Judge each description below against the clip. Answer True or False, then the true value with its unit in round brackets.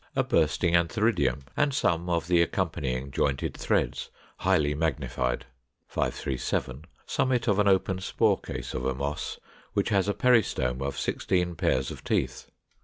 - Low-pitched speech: True (80 Hz)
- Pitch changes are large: True (6.0 semitones)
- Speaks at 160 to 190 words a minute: False (145 wpm)